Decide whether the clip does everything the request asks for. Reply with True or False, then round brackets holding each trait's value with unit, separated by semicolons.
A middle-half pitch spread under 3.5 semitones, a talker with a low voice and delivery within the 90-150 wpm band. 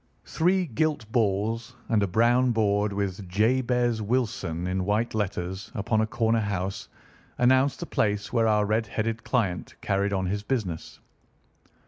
True (2.9 semitones; 110 Hz; 145 wpm)